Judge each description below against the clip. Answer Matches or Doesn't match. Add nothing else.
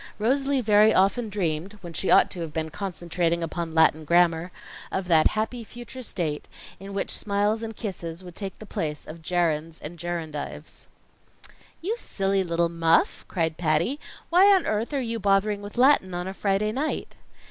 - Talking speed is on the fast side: Doesn't match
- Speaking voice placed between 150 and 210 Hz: Matches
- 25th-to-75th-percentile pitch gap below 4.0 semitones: Doesn't match